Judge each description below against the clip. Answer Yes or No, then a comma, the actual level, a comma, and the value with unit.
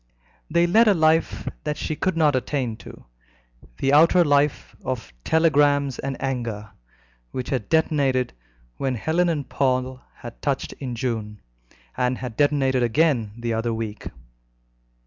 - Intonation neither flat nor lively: Yes, average, 4.2 semitones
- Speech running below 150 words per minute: Yes, average, 140 wpm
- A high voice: No, low, 135 Hz